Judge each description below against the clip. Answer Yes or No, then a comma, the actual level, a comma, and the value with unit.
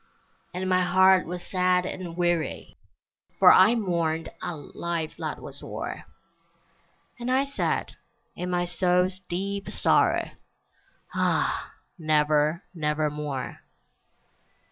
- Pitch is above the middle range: No, medium, 175 Hz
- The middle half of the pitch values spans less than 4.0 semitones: Yes, average, 2.8 semitones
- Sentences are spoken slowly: Yes, slow, 105 wpm